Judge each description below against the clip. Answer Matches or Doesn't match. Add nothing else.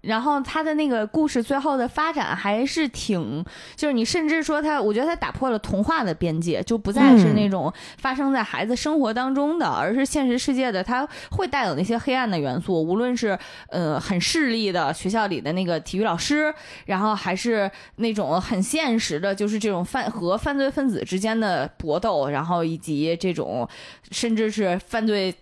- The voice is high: Matches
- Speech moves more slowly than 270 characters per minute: Doesn't match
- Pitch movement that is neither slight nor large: Doesn't match